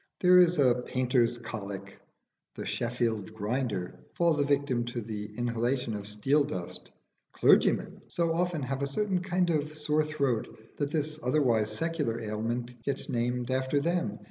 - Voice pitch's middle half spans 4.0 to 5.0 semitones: Yes, average, 4.7 semitones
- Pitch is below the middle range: Yes, low, 130 Hz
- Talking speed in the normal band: Yes, average, 150 wpm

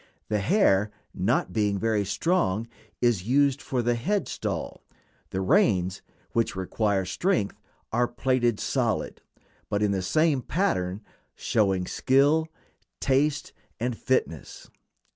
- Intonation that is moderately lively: No, wide, 6.1 semitones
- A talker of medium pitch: No, low, 115 Hz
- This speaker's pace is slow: Yes, slow, 120 wpm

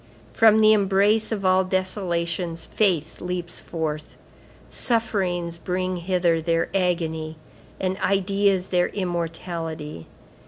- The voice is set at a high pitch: No, medium, 180 Hz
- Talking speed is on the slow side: Yes, slow, 105 wpm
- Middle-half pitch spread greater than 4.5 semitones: No, narrow, 2.5 semitones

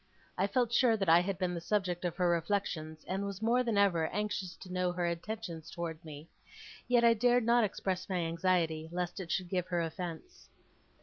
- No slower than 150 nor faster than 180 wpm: No, average, 200 wpm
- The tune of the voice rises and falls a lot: No, average, 3.5 semitones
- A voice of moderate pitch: Yes, medium, 180 Hz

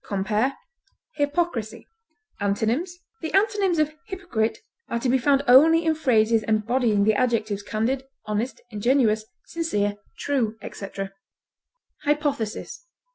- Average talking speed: No, slow, 110 wpm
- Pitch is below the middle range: No, high, 245 Hz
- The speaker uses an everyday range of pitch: No, wide, 5.8 semitones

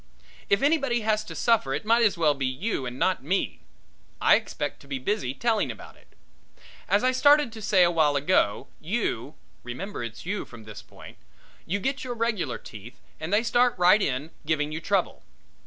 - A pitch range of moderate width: No, wide, 8.5 semitones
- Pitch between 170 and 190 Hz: Yes, medium, 185 Hz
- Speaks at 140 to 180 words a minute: No, average, 190 wpm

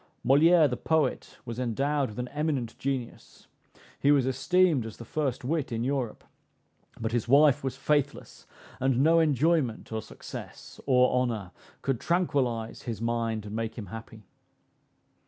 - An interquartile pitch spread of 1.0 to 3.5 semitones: No, average, 4.0 semitones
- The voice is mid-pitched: No, low, 130 Hz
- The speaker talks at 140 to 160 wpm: Yes, average, 150 wpm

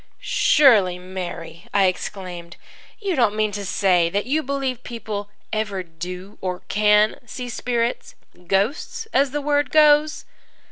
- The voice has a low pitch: No, high, 210 Hz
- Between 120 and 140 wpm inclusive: Yes, slow, 135 wpm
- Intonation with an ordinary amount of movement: No, wide, 6.5 semitones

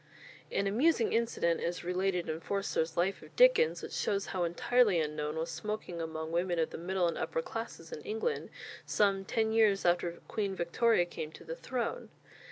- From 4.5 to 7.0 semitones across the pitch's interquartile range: Yes, average, 4.9 semitones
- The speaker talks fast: No, average, 175 wpm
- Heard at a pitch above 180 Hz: Yes, high, 190 Hz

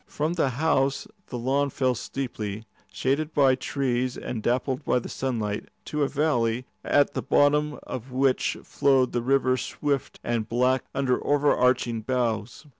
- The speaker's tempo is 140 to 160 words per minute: Yes, average, 150 wpm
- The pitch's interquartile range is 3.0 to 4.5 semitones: No, narrow, 2.6 semitones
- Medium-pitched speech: No, low, 130 Hz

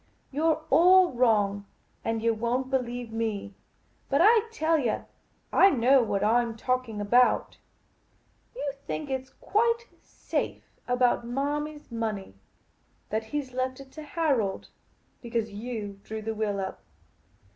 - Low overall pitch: No, high, 245 Hz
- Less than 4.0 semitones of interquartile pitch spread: No, average, 4.7 semitones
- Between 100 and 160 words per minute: Yes, average, 155 wpm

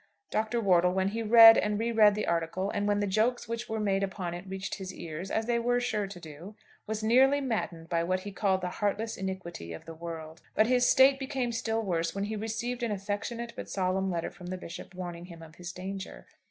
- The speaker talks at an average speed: No, fast, 230 wpm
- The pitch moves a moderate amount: Yes, average, 3.9 semitones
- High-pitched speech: Yes, high, 200 Hz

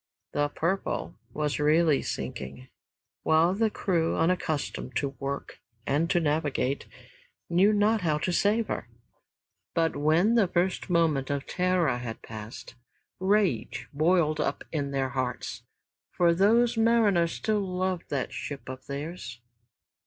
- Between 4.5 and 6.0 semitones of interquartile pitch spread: Yes, average, 4.9 semitones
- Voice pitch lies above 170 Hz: No, medium, 165 Hz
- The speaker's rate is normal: No, slow, 130 wpm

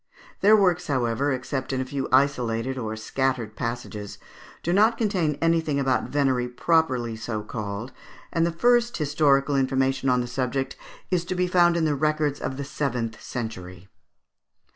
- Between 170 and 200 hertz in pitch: No, low, 135 Hz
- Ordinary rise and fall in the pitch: Yes, average, 4.8 semitones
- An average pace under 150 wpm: No, average, 160 wpm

